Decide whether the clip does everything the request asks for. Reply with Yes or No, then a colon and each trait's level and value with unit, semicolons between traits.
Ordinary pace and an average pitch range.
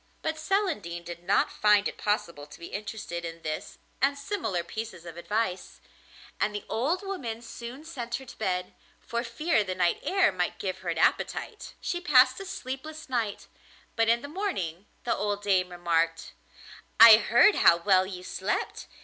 No: average, 175 wpm; wide, 6.7 semitones